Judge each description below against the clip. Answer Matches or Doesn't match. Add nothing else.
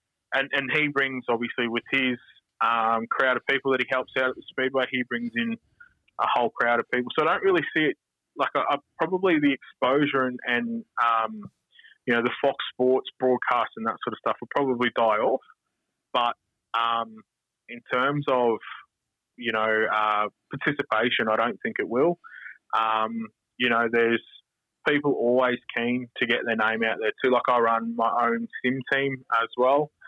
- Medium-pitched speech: Doesn't match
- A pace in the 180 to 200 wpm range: Matches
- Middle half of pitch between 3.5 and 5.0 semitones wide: Doesn't match